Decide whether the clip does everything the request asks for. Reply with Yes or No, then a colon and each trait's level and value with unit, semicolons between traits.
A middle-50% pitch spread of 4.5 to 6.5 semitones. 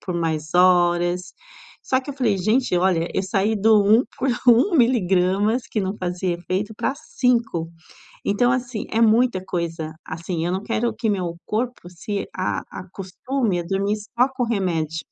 Yes: average, 4.8 semitones